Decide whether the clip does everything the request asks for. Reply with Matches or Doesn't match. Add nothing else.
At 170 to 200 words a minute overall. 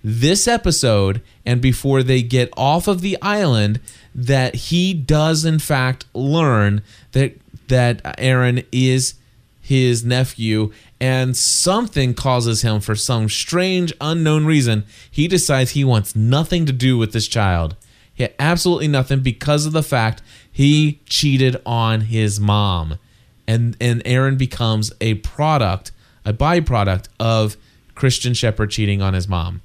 Doesn't match